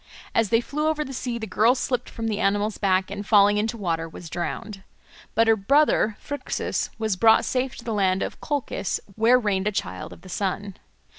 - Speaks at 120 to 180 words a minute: No, fast, 205 wpm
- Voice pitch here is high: Yes, high, 215 Hz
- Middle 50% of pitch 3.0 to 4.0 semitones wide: Yes, average, 3.4 semitones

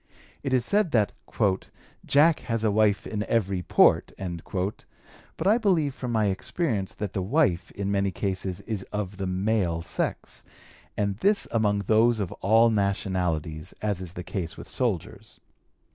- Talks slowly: No, average, 155 wpm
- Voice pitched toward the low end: Yes, low, 100 Hz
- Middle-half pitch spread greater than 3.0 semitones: Yes, average, 3.5 semitones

